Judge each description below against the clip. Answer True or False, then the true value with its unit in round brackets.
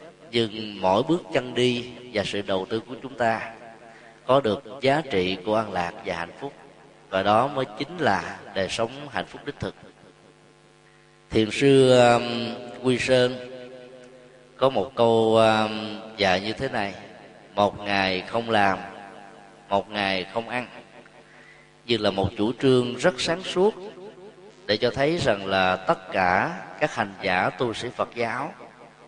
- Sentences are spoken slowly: True (155 wpm)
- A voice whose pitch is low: True (115 Hz)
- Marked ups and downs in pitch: False (3.9 semitones)